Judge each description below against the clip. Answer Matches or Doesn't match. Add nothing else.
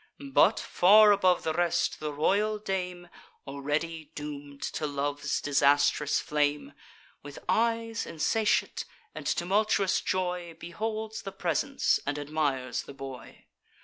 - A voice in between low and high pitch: Matches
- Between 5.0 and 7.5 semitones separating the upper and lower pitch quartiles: Matches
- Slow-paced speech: Matches